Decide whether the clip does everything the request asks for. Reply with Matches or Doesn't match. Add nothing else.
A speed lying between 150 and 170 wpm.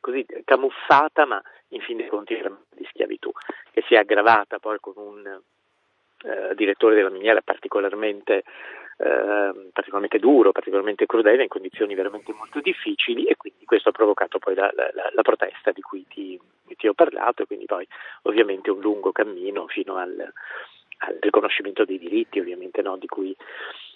Matches